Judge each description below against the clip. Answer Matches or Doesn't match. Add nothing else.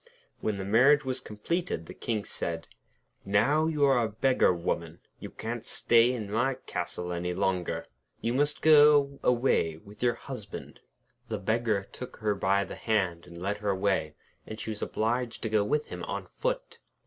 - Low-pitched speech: Matches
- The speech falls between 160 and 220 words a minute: Matches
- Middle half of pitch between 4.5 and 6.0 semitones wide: Matches